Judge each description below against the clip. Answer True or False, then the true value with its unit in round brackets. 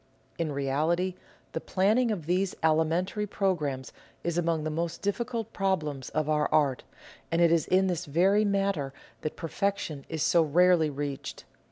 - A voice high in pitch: False (170 Hz)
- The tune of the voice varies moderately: True (4.0 semitones)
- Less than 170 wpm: True (155 wpm)